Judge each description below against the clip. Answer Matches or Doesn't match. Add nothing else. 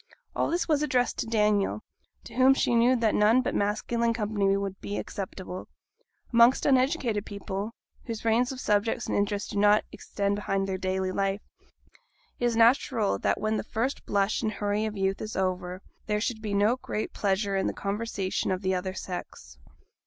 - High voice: Matches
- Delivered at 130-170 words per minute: Doesn't match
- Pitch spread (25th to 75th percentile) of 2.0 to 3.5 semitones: Matches